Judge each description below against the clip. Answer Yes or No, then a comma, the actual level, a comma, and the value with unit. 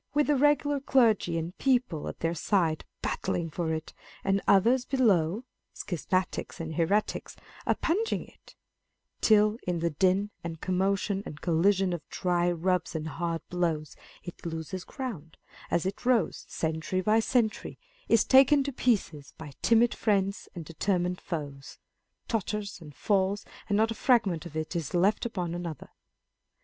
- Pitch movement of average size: Yes, average, 4.7 semitones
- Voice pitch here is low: No, medium, 185 Hz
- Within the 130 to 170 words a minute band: Yes, average, 150 wpm